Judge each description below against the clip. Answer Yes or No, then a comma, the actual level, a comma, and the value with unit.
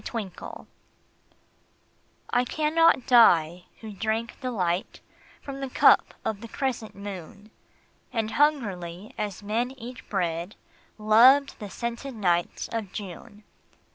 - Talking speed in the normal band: No, slow, 115 wpm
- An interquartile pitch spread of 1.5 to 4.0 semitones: No, average, 4.4 semitones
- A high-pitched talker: Yes, high, 220 Hz